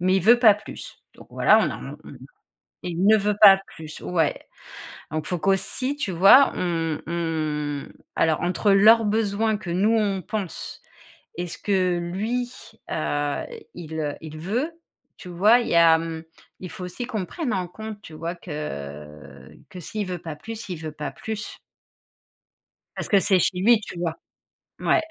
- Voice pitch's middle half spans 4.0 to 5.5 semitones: Yes, average, 4.7 semitones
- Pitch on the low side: No, medium, 180 Hz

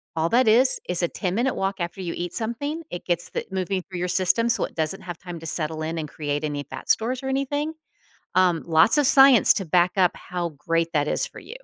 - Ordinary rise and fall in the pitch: No, wide, 5.7 semitones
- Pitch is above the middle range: No, medium, 180 Hz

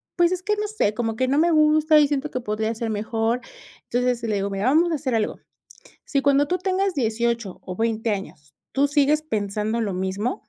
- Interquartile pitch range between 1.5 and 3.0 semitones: No, wide, 5.8 semitones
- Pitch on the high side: Yes, high, 245 Hz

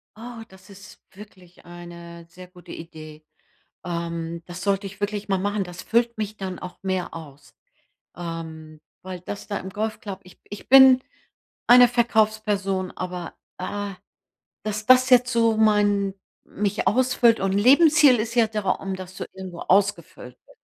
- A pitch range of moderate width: Yes, average, 3.4 semitones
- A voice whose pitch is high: Yes, high, 195 Hz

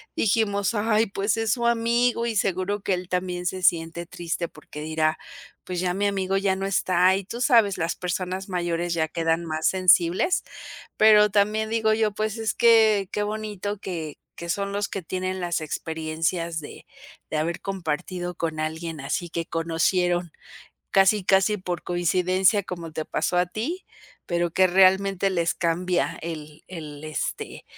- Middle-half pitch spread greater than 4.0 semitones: No, average, 3.3 semitones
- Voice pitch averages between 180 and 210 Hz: Yes, medium, 185 Hz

